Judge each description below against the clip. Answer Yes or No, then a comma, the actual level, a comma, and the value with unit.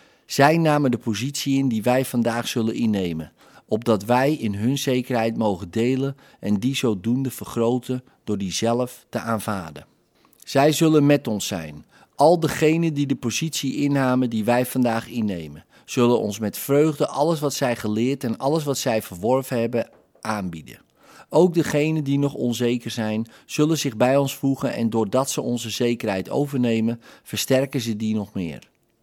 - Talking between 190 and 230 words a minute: No, average, 160 wpm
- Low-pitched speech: Yes, low, 120 Hz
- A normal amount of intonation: Yes, average, 3.8 semitones